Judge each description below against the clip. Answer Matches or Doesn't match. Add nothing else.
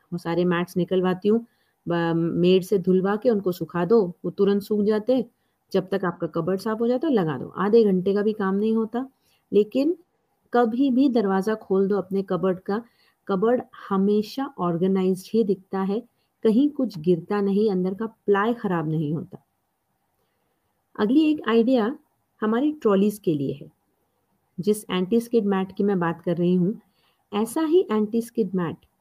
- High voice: Matches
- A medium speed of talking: Matches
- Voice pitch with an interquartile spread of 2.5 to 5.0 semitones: Matches